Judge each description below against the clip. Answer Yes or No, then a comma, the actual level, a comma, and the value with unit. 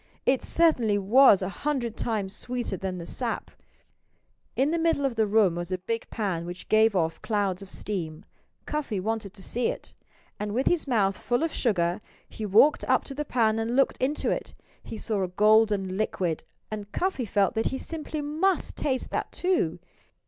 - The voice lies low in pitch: No, high, 220 Hz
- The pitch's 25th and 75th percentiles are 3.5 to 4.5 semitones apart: No, average, 5.3 semitones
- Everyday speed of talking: Yes, average, 185 wpm